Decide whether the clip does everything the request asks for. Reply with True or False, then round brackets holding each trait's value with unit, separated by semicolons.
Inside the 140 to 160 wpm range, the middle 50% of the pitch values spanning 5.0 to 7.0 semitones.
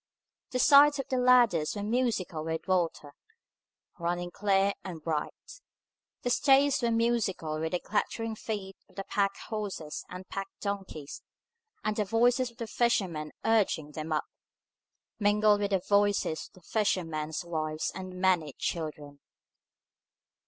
True (145 wpm; 5.6 semitones)